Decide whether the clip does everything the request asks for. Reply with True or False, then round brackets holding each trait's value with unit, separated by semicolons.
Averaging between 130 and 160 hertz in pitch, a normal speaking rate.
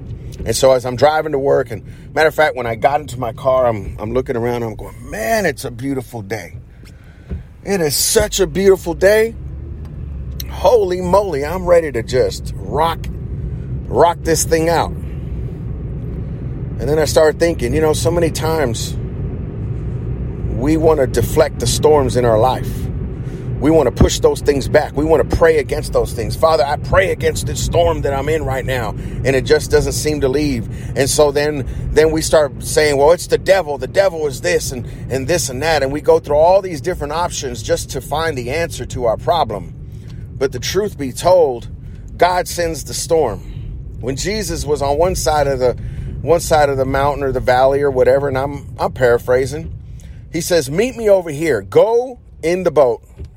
True (140 Hz; 195 wpm)